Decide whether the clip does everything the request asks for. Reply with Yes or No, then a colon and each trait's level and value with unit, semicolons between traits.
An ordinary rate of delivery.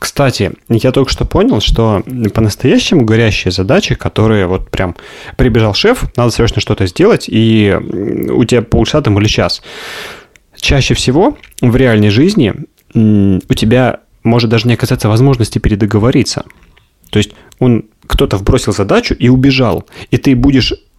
Yes: average, 140 wpm